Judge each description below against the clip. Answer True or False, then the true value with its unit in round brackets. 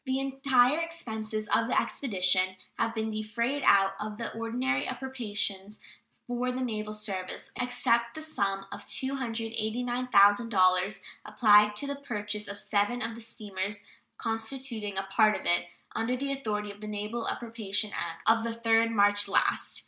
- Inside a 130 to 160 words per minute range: True (150 wpm)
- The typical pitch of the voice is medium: False (225 Hz)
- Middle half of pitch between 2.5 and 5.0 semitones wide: True (3.1 semitones)